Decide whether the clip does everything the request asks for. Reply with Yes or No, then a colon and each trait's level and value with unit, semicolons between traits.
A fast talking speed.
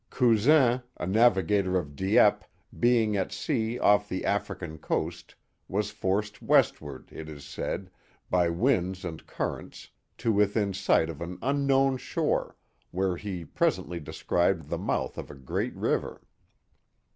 No: average, 140 wpm